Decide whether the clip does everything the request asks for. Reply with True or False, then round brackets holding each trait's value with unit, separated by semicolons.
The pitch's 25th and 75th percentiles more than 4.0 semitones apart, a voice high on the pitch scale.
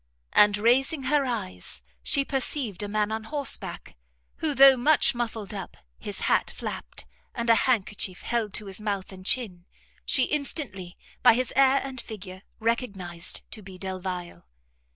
True (5.4 semitones; 220 Hz)